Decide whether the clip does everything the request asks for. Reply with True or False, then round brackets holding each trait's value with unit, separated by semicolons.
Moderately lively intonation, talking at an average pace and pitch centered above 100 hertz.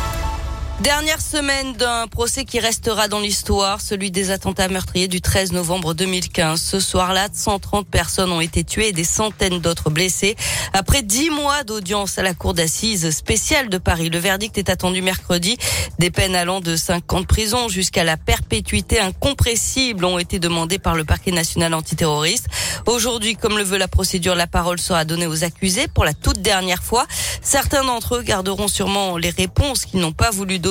True (3.5 semitones; 180 wpm; 190 Hz)